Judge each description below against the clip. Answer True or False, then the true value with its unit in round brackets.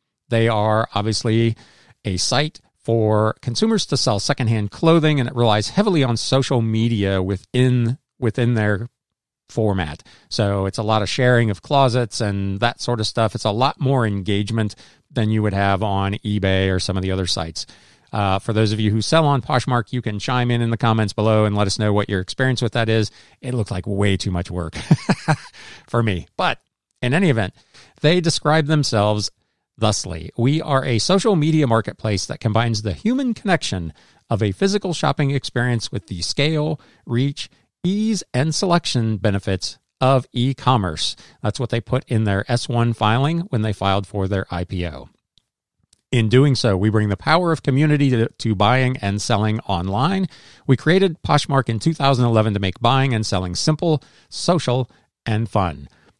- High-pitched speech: False (115 Hz)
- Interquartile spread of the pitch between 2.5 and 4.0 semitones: False (4.5 semitones)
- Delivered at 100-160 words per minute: False (175 wpm)